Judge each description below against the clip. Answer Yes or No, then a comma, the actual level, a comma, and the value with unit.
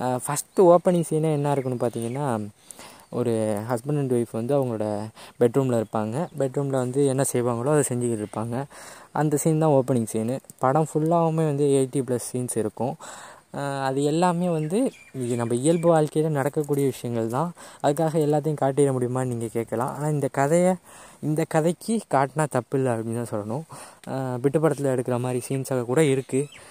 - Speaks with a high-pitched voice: No, low, 135 Hz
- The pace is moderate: No, fast, 145 wpm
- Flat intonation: No, average, 4.0 semitones